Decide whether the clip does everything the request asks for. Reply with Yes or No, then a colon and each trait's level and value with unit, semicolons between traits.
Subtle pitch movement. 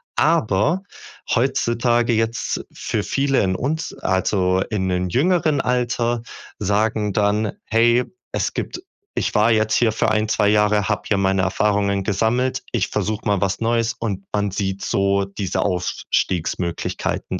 No: average, 3.2 semitones